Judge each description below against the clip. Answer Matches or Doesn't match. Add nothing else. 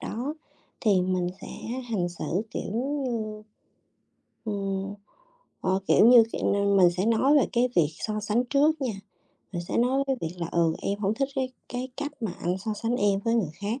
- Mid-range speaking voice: Doesn't match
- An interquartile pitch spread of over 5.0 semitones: Doesn't match